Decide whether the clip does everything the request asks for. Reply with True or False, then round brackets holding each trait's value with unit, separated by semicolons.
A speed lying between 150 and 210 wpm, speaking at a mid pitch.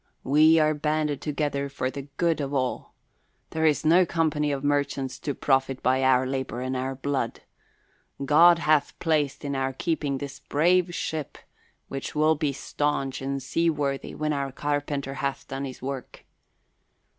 True (160 wpm; 145 Hz)